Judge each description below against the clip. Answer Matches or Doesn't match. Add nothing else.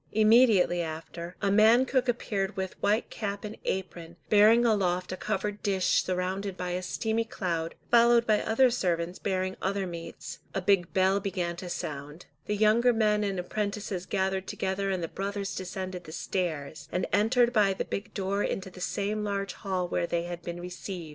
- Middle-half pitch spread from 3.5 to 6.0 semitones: Doesn't match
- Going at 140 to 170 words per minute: Doesn't match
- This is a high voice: Matches